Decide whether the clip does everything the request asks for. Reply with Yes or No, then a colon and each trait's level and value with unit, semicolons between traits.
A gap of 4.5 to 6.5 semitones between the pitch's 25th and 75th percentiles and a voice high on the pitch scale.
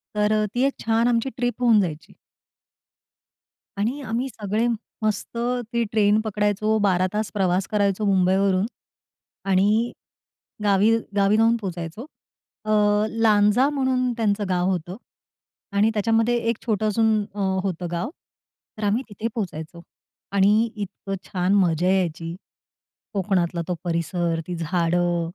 No: average, 3.4 semitones; high, 205 Hz